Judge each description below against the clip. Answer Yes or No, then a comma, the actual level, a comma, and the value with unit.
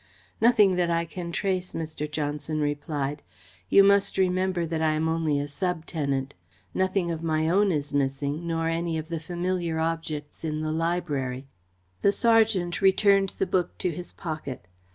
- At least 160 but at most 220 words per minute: Yes, average, 165 wpm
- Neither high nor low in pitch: Yes, medium, 165 Hz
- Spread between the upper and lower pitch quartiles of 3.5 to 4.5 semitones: No, average, 3.1 semitones